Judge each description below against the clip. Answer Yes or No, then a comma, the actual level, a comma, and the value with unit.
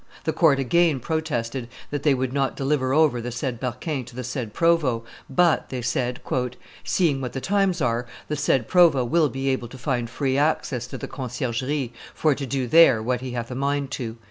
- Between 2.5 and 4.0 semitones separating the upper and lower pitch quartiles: Yes, average, 3.4 semitones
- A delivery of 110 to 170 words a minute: No, average, 200 wpm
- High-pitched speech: No, low, 130 Hz